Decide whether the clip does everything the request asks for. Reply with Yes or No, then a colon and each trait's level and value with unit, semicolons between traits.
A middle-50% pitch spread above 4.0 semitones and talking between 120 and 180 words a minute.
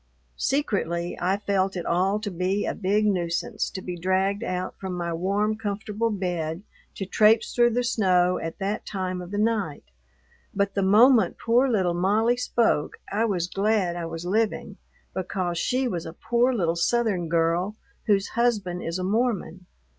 No: average, 3.5 semitones; average, 170 wpm